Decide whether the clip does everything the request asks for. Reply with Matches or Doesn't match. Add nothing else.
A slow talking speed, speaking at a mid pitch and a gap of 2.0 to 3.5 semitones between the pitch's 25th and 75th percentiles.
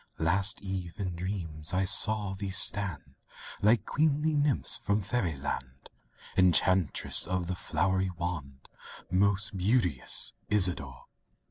Doesn't match